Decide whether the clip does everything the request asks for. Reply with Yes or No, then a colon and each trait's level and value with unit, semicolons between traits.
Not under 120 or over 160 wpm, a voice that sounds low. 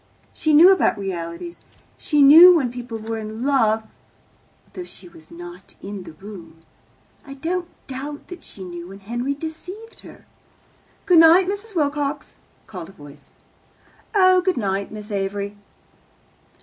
No: average, 145 wpm; high, 240 Hz